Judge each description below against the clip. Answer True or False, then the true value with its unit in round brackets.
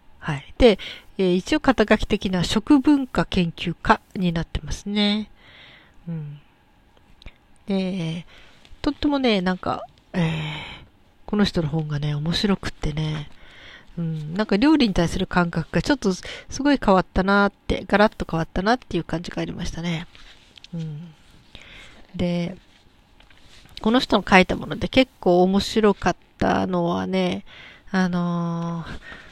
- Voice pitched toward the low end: False (185 Hz)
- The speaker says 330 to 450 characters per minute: False (260 characters per minute)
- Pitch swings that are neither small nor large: True (3.8 semitones)